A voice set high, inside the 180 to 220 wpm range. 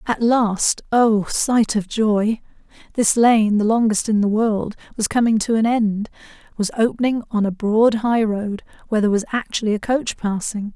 No: high, 220 Hz; average, 160 wpm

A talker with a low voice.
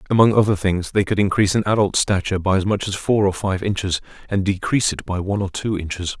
Yes: low, 100 Hz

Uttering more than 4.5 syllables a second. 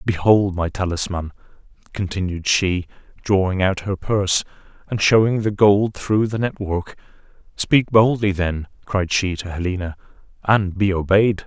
No: 4.4 syllables/s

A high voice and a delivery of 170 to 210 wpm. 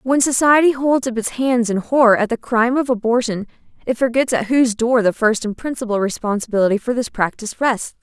Yes: high, 235 Hz; average, 200 wpm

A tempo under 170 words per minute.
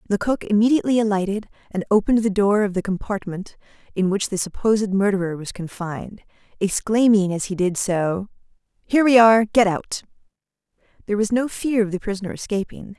Yes: average, 160 wpm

